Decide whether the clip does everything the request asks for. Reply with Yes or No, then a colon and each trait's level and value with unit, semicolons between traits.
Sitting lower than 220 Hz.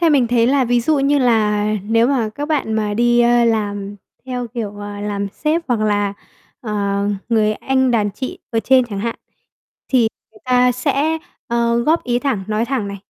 No: high, 235 Hz